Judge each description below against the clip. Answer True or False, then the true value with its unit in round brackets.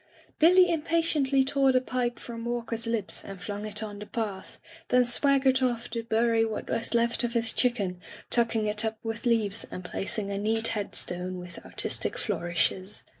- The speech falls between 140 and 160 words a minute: False (180 wpm)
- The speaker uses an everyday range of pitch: True (3.2 semitones)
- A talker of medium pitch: False (230 Hz)